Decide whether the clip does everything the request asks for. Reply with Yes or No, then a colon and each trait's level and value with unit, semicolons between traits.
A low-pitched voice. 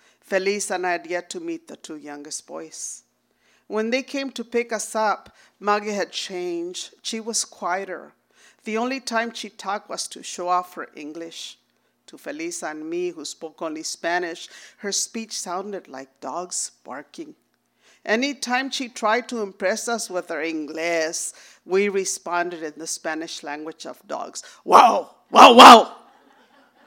No: high, 200 Hz